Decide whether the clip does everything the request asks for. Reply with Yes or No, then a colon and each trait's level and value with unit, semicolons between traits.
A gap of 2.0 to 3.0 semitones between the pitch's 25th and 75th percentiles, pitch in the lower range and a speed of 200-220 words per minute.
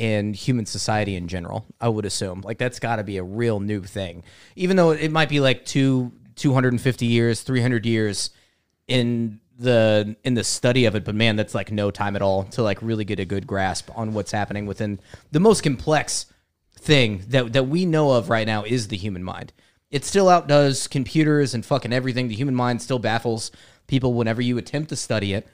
No: average, 4.1 semitones; low, 115 Hz; fast, 205 wpm